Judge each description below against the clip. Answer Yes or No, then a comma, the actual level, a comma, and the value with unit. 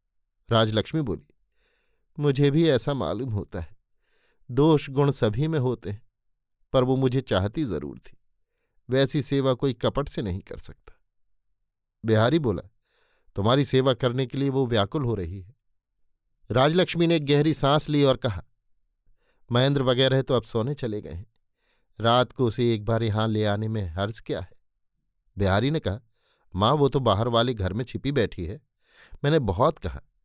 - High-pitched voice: No, low, 120 Hz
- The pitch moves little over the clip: No, average, 5.2 semitones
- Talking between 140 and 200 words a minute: Yes, average, 165 wpm